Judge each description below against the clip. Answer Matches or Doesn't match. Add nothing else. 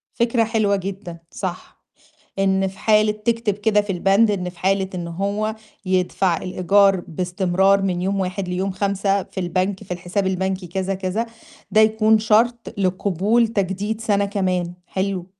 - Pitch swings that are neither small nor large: Doesn't match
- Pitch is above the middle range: Matches